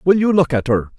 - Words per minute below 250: No, fast, 305 wpm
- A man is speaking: Yes, male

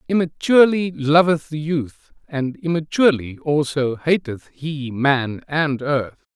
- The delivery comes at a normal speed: No, slow, 115 wpm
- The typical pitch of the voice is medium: Yes, medium, 150 Hz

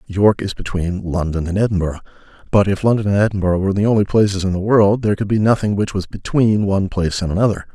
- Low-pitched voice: Yes, low, 100 Hz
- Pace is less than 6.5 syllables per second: No, 6.6 syllables/s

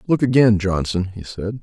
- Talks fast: No, average, 185 wpm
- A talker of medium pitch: No, low, 105 Hz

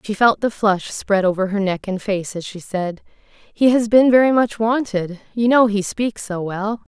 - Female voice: Yes, female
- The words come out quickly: Yes, fast, 215 wpm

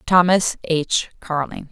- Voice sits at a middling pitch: Yes, medium, 165 Hz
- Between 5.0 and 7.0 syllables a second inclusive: No, 3.5 syllables/s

